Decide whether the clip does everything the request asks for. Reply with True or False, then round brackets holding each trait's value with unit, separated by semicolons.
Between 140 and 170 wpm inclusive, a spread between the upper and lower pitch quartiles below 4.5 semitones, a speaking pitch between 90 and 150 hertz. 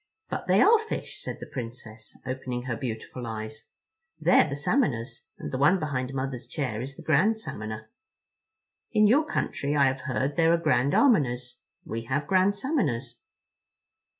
False (160 wpm; 5.5 semitones; 135 Hz)